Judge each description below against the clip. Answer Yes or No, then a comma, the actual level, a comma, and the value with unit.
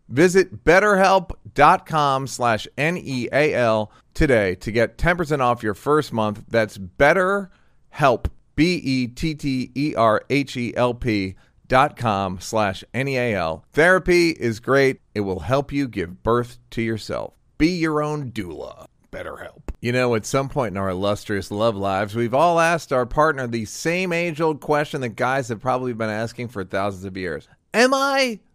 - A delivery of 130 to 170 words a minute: Yes, average, 140 wpm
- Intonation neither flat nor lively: No, wide, 5.8 semitones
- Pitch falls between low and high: No, low, 125 Hz